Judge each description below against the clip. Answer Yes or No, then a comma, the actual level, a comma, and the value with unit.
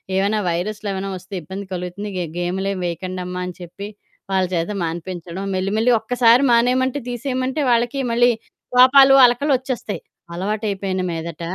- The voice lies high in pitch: Yes, high, 200 Hz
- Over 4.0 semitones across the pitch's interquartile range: Yes, average, 5.1 semitones